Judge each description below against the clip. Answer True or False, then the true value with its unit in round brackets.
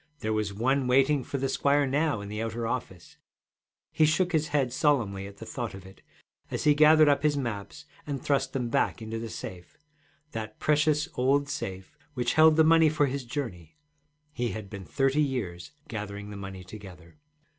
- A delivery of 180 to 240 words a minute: True (185 wpm)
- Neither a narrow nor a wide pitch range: False (6.1 semitones)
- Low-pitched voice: True (125 Hz)